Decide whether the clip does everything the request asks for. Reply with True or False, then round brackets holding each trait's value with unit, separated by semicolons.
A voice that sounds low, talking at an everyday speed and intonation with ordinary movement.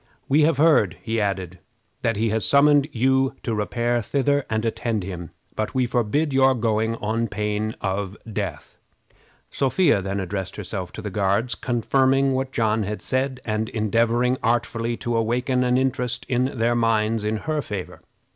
True (115 Hz; 160 wpm; 3.6 semitones)